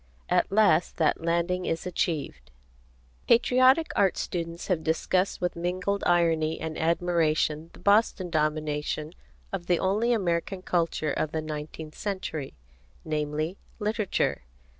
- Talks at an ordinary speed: No, slow, 120 wpm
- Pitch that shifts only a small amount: No, average, 3.2 semitones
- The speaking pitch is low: No, medium, 170 Hz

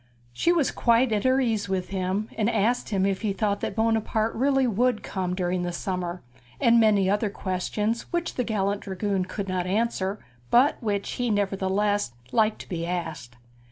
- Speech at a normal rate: Yes, average, 180 wpm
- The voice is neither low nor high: No, high, 205 Hz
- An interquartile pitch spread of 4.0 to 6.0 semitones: No, average, 3.3 semitones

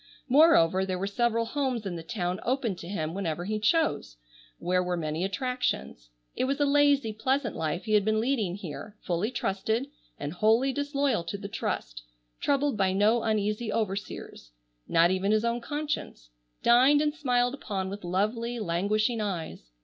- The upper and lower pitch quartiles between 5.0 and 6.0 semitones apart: Yes, average, 5.3 semitones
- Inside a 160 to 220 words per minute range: Yes, average, 165 wpm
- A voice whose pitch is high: Yes, high, 215 Hz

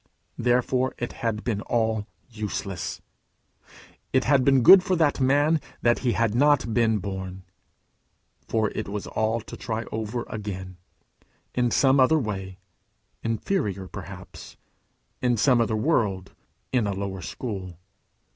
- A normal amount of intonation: Yes, average, 4.0 semitones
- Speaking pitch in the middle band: No, low, 115 Hz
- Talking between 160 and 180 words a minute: No, slow, 135 wpm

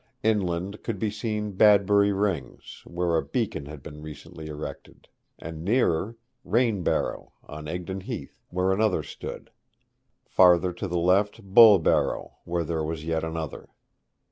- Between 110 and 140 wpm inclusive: Yes, slow, 135 wpm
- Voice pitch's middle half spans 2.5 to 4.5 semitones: Yes, average, 4.0 semitones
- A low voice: Yes, very low, 90 Hz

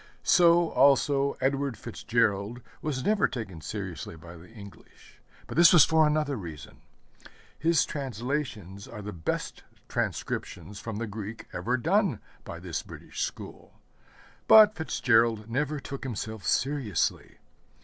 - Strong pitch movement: Yes, wide, 6.0 semitones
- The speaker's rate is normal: No, slow, 130 wpm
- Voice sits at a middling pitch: No, low, 125 Hz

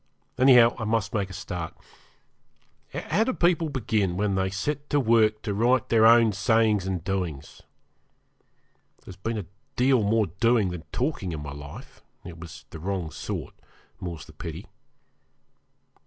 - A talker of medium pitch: No, low, 105 Hz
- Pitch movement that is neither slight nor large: Yes, average, 4.4 semitones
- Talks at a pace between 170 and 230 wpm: No, average, 155 wpm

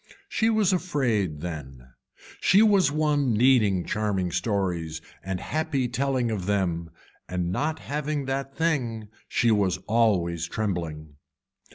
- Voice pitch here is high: No, low, 110 Hz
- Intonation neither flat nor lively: No, wide, 8.0 semitones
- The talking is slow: Yes, slow, 125 wpm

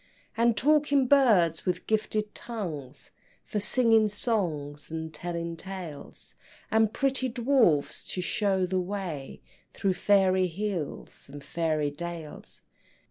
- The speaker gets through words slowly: Yes, slow, 115 wpm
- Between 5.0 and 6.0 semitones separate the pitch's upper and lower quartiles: Yes, average, 5.3 semitones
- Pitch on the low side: No, high, 190 Hz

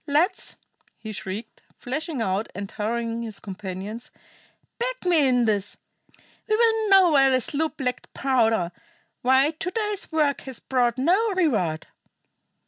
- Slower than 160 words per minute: Yes, average, 140 wpm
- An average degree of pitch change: No, wide, 7.4 semitones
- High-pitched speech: Yes, very high, 260 Hz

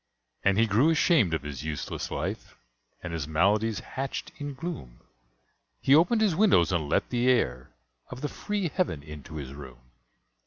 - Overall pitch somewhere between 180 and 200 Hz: No, low, 105 Hz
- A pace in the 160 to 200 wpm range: Yes, average, 165 wpm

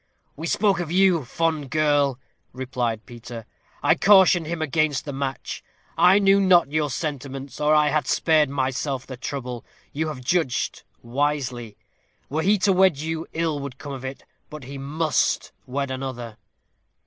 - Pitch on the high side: No, medium, 145 Hz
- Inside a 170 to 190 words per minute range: No, average, 160 wpm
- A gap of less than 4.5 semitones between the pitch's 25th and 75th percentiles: Yes, average, 3.6 semitones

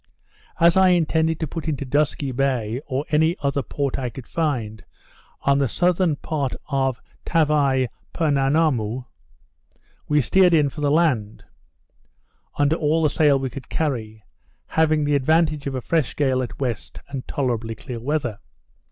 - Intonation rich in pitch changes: No, average, 3.4 semitones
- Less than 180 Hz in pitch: Yes, medium, 140 Hz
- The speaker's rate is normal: Yes, average, 150 wpm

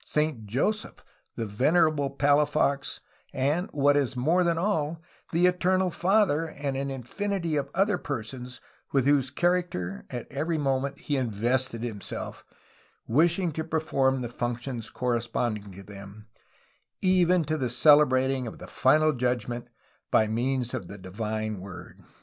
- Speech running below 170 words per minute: Yes, slow, 135 wpm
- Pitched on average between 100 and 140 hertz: Yes, low, 135 Hz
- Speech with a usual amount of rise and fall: Yes, average, 4.9 semitones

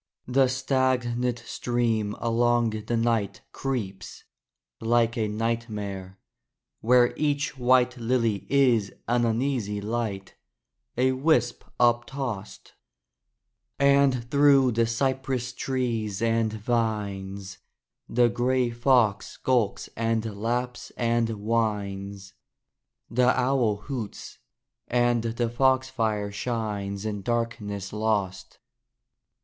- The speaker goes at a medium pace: No, slow, 95 wpm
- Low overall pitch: Yes, low, 115 Hz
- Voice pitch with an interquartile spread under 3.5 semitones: Yes, average, 2.8 semitones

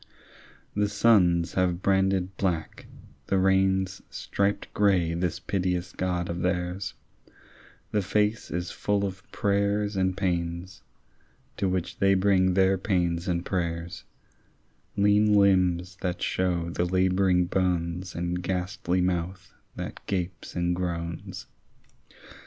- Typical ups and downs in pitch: No, narrow, 1.7 semitones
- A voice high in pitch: No, very low, 90 Hz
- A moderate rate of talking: No, slow, 120 wpm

